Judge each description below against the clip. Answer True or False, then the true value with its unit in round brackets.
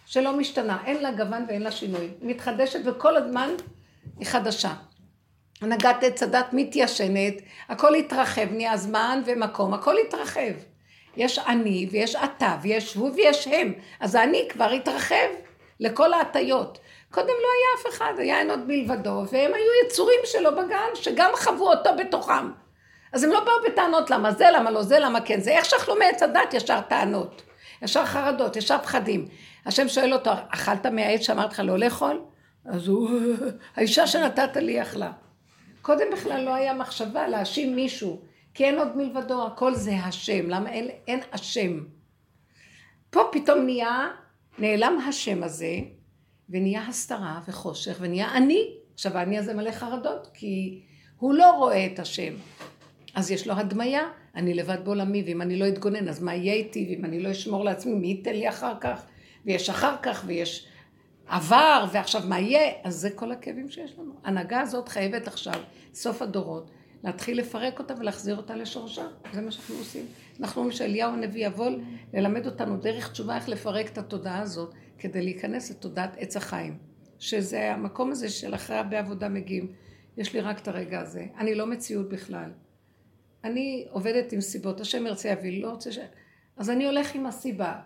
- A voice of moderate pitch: False (225 Hz)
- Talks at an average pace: False (165 wpm)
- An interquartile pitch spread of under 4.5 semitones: False (5.1 semitones)